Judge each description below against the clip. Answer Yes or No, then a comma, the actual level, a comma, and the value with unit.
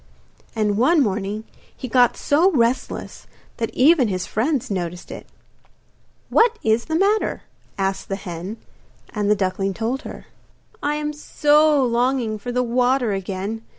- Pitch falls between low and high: No, high, 235 Hz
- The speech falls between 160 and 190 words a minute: No, average, 145 wpm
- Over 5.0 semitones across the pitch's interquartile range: Yes, wide, 5.6 semitones